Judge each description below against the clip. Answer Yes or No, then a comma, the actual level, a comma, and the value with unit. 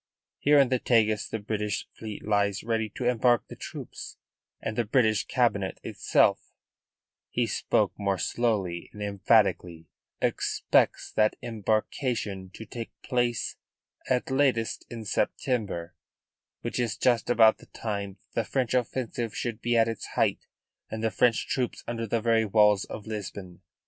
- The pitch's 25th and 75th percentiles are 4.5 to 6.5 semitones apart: No, narrow, 2.5 semitones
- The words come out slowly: No, average, 150 wpm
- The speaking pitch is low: Yes, low, 110 Hz